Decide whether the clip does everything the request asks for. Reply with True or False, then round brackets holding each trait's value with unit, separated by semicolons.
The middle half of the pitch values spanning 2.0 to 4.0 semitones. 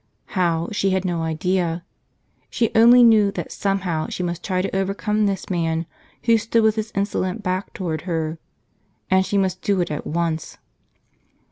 True (3.2 semitones)